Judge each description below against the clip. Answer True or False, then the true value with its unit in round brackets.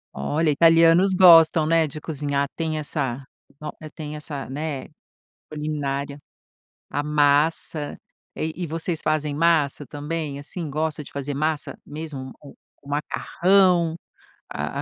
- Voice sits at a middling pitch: True (150 Hz)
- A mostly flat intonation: True (2.2 semitones)